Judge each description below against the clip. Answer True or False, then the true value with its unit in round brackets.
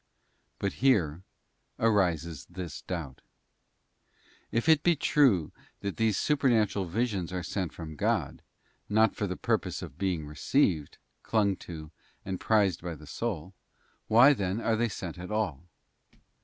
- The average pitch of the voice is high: False (95 Hz)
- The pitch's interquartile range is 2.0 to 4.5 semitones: False (4.9 semitones)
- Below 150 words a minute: True (140 wpm)